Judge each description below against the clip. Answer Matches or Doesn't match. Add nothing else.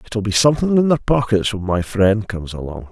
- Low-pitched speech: Matches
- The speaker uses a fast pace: Matches